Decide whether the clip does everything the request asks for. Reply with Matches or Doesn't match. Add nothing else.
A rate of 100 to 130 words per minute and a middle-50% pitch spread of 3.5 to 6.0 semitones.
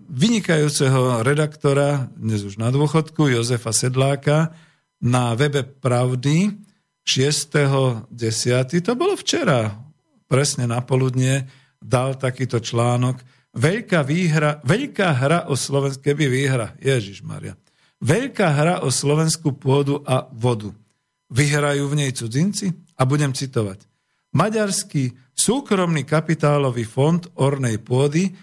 Matches